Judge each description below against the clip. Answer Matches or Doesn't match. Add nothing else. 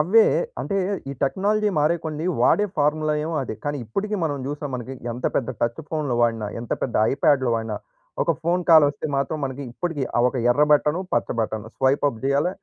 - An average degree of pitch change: Matches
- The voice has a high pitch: Doesn't match